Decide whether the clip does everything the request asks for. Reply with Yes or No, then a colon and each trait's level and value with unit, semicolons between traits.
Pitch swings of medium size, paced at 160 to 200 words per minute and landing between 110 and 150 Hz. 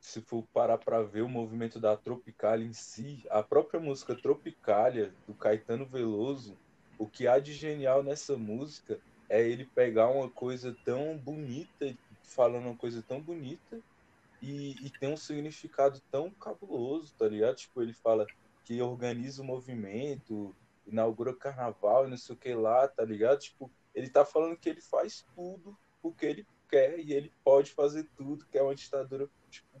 Yes: average, 4.1 semitones; average, 170 wpm; low, 135 Hz